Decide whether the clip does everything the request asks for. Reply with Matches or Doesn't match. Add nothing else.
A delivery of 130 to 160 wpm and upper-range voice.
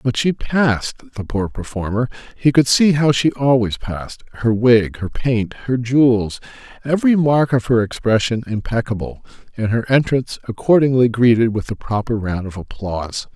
Doesn't match